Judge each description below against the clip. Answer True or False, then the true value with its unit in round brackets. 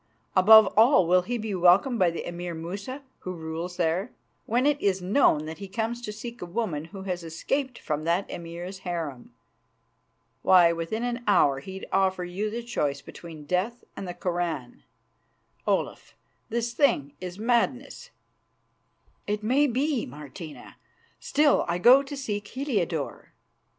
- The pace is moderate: True (150 wpm)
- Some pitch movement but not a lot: False (5.7 semitones)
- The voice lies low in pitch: False (190 Hz)